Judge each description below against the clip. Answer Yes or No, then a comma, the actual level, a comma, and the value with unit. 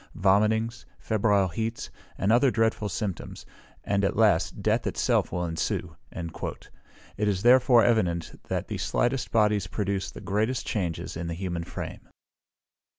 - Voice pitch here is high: No, low, 105 Hz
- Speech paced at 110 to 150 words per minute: Yes, average, 140 wpm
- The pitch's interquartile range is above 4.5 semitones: No, average, 3.8 semitones